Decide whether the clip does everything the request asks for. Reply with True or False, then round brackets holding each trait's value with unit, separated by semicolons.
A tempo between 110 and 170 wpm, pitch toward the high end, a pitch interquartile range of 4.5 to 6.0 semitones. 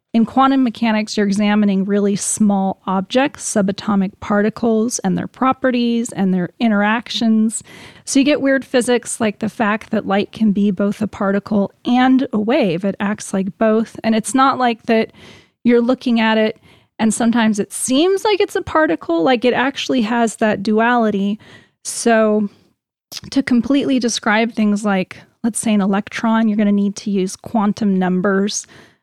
False (165 wpm; 220 Hz; 3.2 semitones)